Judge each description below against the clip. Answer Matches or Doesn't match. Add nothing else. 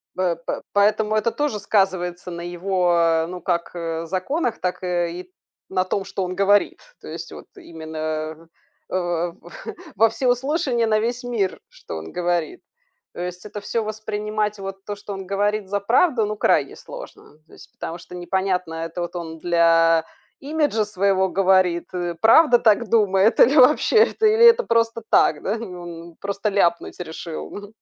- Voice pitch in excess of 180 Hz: Matches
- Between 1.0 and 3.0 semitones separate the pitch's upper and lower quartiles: Doesn't match